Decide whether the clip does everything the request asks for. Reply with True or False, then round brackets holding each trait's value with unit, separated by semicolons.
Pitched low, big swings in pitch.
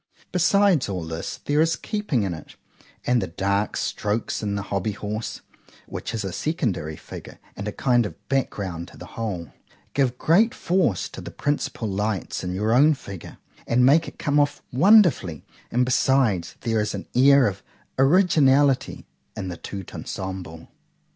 True (115 Hz; 6.6 semitones)